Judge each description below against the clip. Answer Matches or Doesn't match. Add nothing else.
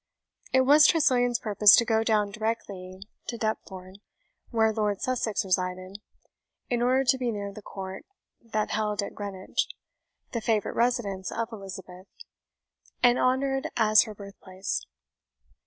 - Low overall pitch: Doesn't match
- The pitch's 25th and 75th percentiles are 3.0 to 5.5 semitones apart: Matches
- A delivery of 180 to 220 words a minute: Doesn't match